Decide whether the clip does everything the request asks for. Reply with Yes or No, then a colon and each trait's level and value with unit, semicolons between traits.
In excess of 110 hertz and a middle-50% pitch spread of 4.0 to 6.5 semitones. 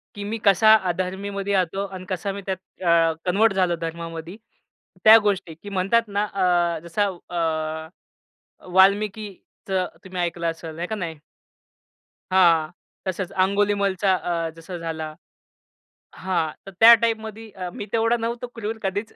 No: high, 190 Hz; average, 3.2 semitones